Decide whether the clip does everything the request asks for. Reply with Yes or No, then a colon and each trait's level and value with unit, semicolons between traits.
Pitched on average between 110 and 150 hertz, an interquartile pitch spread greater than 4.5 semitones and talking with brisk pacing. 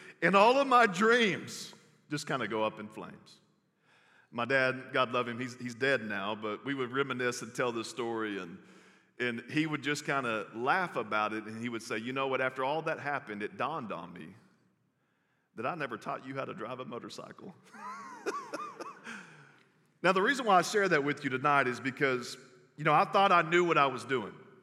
Yes: low, 135 Hz; average, 5.2 semitones; fast, 210 wpm